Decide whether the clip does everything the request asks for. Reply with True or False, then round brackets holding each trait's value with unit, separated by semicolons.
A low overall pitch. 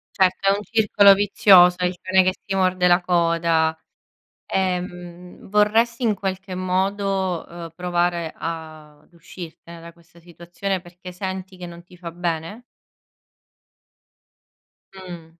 False (180 Hz)